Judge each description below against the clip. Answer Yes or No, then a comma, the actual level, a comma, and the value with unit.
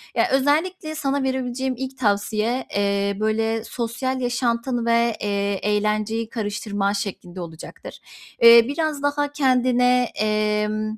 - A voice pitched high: Yes, high, 230 Hz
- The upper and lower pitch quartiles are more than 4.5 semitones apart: No, average, 3.6 semitones